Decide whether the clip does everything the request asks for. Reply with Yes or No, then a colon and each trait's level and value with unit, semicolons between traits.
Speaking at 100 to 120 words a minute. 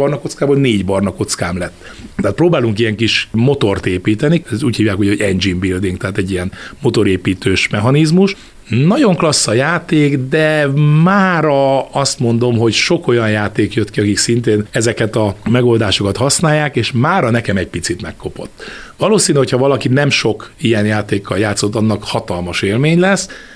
No: fast, 155 wpm